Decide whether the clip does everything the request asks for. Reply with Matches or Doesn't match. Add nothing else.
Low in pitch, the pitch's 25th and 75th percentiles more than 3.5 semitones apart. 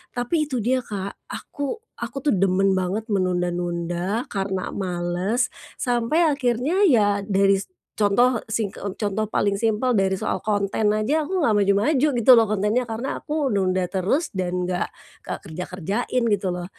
Doesn't match